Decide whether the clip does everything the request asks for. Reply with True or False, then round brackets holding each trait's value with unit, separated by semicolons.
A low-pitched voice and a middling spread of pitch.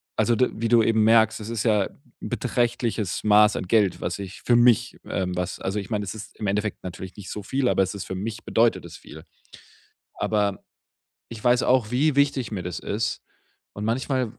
True (110 Hz; 3.2 semitones)